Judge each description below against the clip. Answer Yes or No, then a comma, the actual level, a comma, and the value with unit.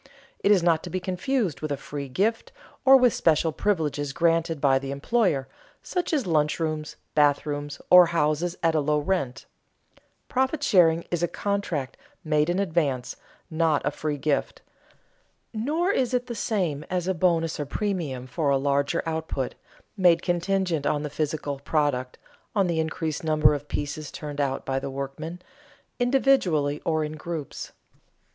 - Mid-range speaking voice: Yes, medium, 160 Hz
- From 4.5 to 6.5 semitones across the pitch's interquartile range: No, average, 4.0 semitones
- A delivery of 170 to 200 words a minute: No, average, 160 wpm